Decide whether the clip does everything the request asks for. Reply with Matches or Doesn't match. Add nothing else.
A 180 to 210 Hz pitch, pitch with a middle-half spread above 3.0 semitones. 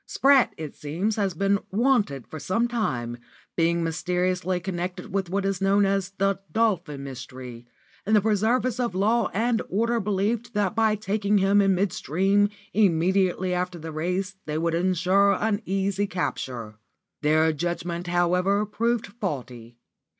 Matches